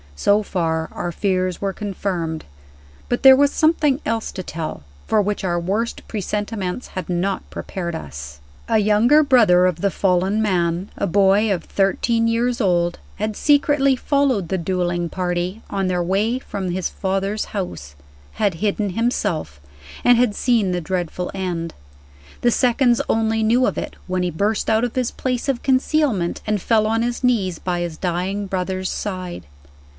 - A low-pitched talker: No, high, 195 Hz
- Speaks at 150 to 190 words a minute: Yes, average, 165 wpm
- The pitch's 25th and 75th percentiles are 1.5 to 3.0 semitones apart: No, average, 4.3 semitones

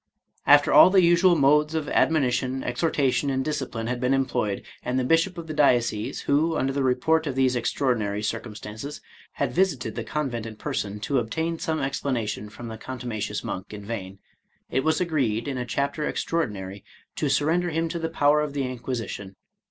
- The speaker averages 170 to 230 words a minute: Yes, average, 180 wpm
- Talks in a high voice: No, low, 130 Hz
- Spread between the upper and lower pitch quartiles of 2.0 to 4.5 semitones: No, average, 5.1 semitones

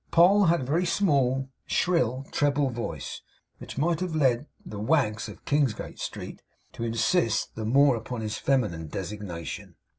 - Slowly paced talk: No, average, 150 wpm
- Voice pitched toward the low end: Yes, low, 130 Hz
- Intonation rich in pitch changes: Yes, wide, 5.8 semitones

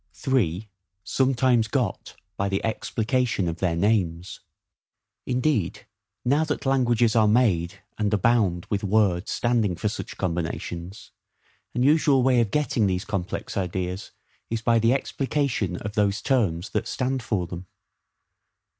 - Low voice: Yes, low, 105 Hz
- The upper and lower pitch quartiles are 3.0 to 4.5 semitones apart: No, average, 5.2 semitones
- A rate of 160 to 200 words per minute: No, slow, 135 wpm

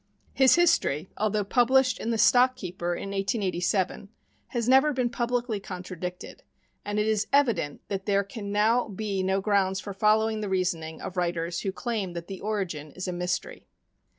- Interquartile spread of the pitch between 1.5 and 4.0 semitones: Yes, average, 3.7 semitones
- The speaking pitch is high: Yes, high, 200 Hz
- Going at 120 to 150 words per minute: No, average, 170 wpm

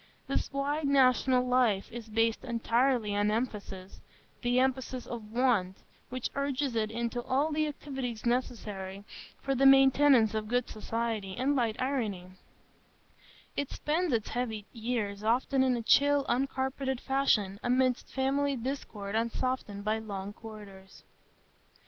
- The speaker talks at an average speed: No, slow, 130 wpm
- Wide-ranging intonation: No, average, 3.7 semitones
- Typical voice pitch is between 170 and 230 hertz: No, high, 245 Hz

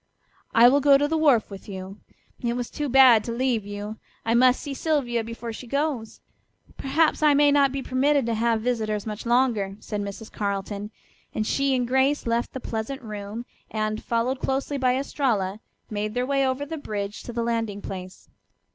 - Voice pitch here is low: No, high, 235 Hz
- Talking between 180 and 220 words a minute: Yes, average, 190 wpm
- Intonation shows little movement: No, average, 4.1 semitones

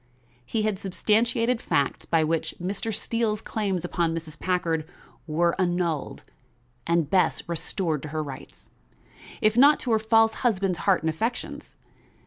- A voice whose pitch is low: No, medium, 185 Hz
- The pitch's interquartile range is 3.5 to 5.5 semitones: Yes, average, 5.1 semitones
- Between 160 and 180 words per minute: No, average, 140 wpm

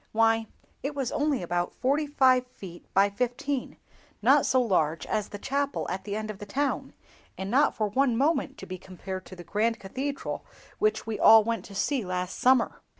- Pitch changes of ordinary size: No, wide, 5.7 semitones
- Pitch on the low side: No, high, 225 Hz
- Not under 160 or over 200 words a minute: Yes, average, 190 wpm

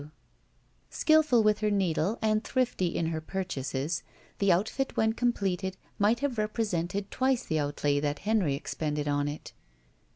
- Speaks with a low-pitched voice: No, high, 190 Hz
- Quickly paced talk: No, average, 155 wpm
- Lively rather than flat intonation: Yes, wide, 6.0 semitones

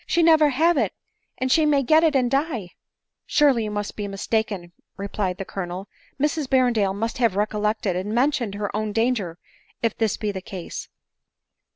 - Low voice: No, high, 220 Hz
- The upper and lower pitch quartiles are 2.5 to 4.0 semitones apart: No, average, 5.2 semitones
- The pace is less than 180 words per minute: No, average, 190 wpm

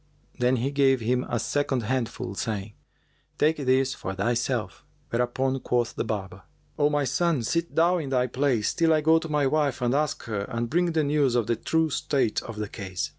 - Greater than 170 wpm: Yes, average, 200 wpm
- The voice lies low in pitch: Yes, low, 130 Hz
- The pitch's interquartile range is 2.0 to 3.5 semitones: No, average, 4.2 semitones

